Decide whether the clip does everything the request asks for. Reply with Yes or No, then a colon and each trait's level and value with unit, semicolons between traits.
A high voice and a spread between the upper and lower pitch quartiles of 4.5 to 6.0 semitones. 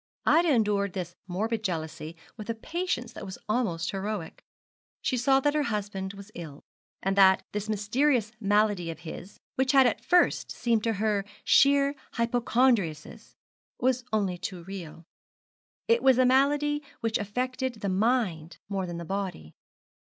Yes: high, 210 Hz; average, 5.0 semitones